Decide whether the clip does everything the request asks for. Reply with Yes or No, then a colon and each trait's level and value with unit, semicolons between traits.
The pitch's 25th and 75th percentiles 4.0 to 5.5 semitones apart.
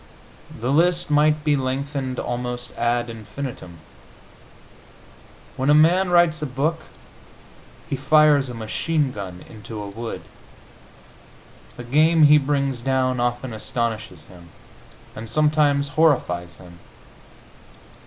Yes: average, 4.4 semitones